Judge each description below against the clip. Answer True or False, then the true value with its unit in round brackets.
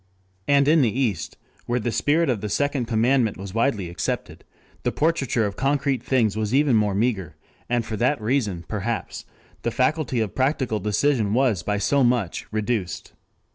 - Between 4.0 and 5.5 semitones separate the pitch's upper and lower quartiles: True (4.5 semitones)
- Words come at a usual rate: True (170 wpm)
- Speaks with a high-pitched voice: False (120 Hz)